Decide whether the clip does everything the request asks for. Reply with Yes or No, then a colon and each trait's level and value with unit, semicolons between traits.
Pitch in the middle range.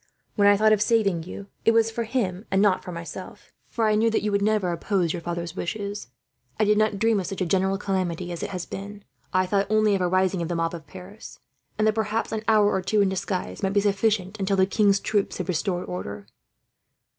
No: high, 195 Hz